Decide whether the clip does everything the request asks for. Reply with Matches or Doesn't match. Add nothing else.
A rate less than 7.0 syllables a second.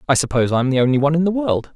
Doesn't match